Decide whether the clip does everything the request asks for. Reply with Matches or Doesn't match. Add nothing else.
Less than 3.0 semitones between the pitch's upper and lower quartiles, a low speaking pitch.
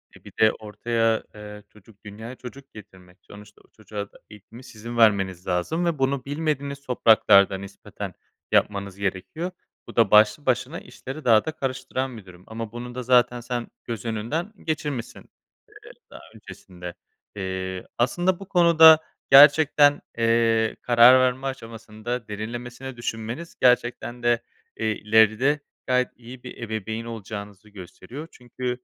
Doesn't match